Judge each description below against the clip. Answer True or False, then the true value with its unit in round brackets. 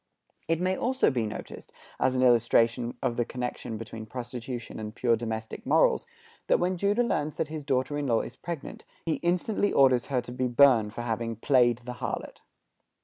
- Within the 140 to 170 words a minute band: False (185 wpm)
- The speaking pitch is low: True (125 Hz)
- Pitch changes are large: False (4.0 semitones)